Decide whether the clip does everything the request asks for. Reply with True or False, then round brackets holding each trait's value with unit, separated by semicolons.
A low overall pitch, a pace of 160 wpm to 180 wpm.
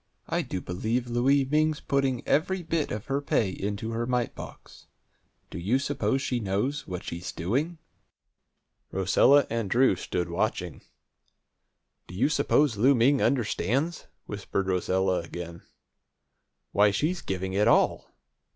False (115 Hz; 135 wpm)